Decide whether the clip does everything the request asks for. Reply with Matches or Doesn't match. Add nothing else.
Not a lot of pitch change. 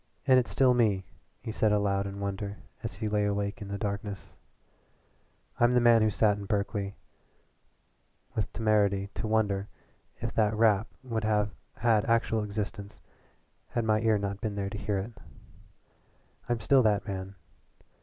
Matches